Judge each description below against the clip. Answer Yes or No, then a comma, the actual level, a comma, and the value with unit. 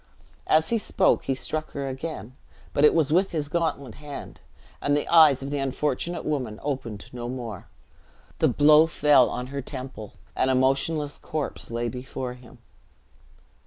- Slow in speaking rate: No, average, 165 wpm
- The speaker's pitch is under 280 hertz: Yes, medium, 140 Hz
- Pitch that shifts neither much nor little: Yes, average, 3.1 semitones